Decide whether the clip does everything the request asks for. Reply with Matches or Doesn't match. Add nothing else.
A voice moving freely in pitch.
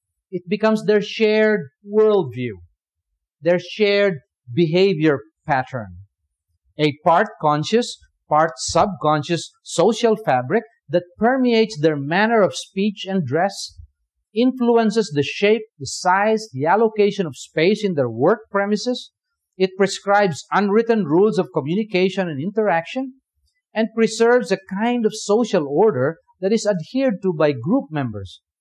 Matches